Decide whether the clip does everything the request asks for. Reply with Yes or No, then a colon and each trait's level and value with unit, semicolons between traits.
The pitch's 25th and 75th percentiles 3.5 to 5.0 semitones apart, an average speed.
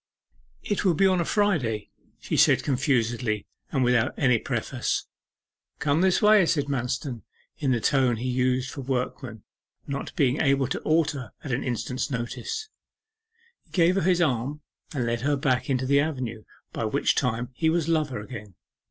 Yes: average, 4.4 semitones; average, 170 wpm